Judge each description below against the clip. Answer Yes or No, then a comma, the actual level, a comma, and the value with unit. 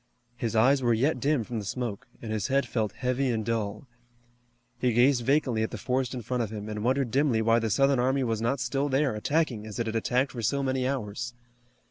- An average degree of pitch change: Yes, average, 3.2 semitones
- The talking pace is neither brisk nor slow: No, fast, 225 wpm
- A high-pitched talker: No, low, 120 Hz